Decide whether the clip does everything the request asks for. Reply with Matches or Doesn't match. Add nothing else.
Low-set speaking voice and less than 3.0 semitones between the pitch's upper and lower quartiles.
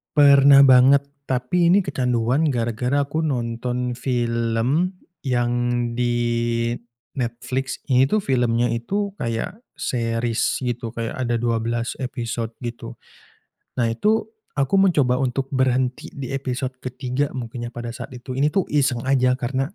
Matches